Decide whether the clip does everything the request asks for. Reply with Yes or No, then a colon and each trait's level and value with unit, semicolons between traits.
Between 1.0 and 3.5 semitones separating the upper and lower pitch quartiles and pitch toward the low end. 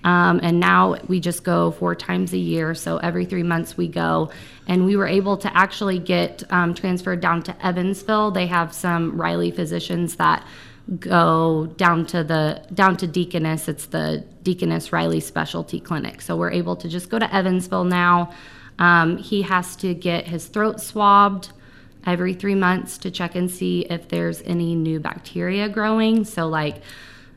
No: average, 2.8 semitones; medium, 175 Hz